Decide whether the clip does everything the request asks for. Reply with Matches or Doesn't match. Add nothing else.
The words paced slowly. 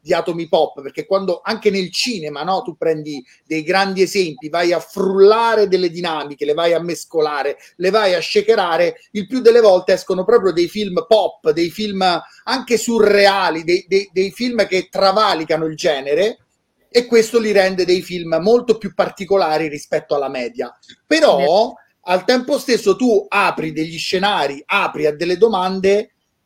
Doesn't match